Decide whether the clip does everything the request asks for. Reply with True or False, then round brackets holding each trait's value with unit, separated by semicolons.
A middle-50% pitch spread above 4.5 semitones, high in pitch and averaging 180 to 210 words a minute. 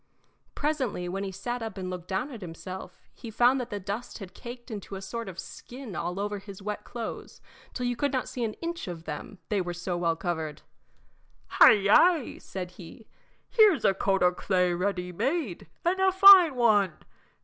True (5.2 semitones; 205 Hz; 190 wpm)